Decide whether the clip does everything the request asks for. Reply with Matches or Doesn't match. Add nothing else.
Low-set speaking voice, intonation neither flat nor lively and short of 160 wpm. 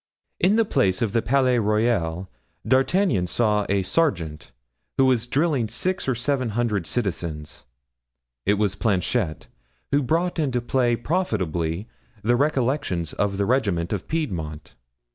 Doesn't match